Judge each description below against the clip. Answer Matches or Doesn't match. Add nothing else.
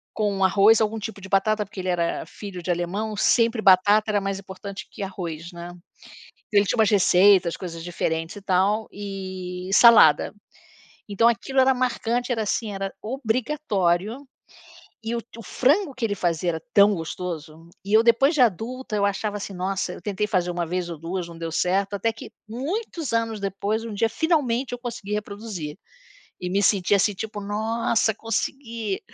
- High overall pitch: Matches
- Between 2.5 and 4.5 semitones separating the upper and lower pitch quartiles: Matches